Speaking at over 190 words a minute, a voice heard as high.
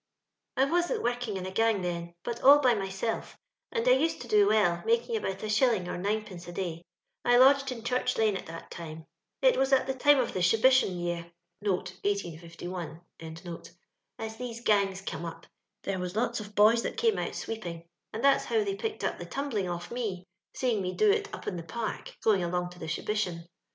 Yes: fast, 205 wpm; high, 210 Hz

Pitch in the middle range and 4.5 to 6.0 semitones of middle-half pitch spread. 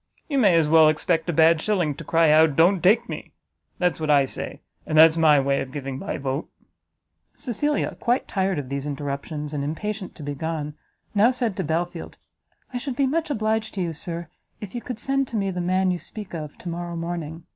Yes: medium, 170 Hz; wide, 5.5 semitones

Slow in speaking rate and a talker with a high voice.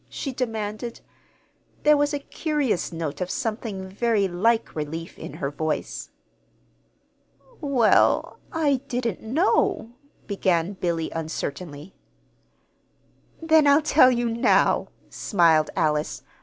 Yes: slow, 105 wpm; high, 215 Hz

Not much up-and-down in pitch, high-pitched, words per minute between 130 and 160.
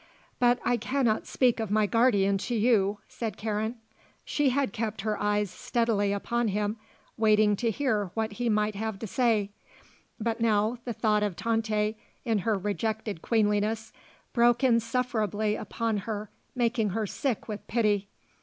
Yes: narrow, 2.1 semitones; high, 220 Hz; average, 155 wpm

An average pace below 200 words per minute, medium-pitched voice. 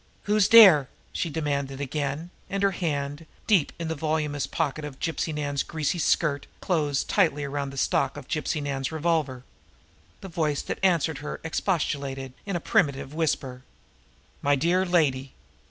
Yes: average, 155 wpm; medium, 150 Hz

